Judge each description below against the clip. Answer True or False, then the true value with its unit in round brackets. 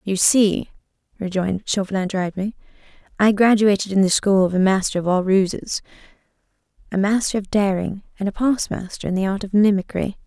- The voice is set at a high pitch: True (195 Hz)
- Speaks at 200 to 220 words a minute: False (165 wpm)